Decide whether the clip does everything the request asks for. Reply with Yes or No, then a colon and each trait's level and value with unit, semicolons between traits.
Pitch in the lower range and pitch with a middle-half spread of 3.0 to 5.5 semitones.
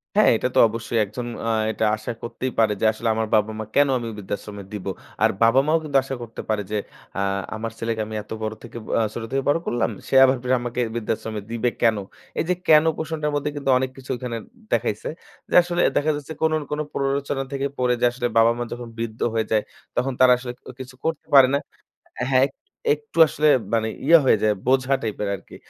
Yes: low, 120 Hz; average, 3.6 semitones